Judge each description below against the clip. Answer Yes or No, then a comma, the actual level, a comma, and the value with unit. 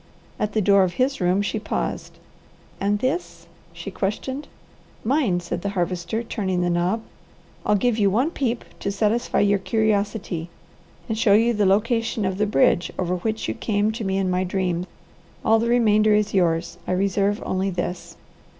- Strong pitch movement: No, average, 3.3 semitones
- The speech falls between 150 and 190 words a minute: Yes, average, 175 wpm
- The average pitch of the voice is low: No, high, 200 Hz